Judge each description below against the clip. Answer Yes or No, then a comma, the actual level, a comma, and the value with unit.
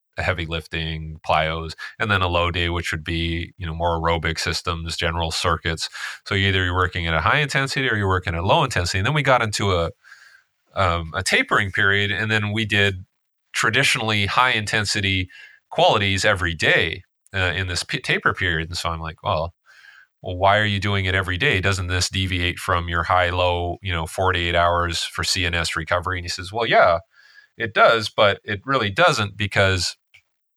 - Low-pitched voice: Yes, very low, 95 Hz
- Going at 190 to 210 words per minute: Yes, average, 195 wpm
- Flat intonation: No, average, 3.3 semitones